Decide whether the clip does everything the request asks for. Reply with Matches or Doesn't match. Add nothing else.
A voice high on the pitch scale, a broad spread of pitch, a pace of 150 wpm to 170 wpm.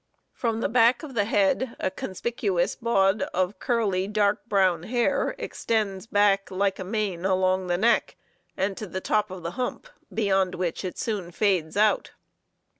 Doesn't match